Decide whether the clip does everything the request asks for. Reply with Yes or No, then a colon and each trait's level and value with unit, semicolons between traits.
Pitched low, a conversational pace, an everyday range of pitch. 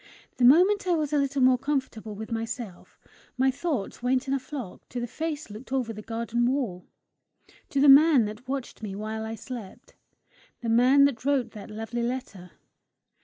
No: very high, 250 Hz; average, 185 wpm; average, 3.7 semitones